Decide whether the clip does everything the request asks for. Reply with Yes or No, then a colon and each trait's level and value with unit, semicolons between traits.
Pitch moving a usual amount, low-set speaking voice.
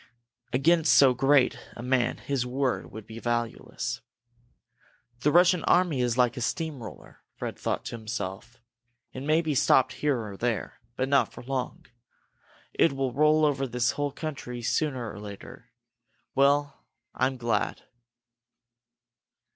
Yes: average, 3.3 semitones; low, 130 Hz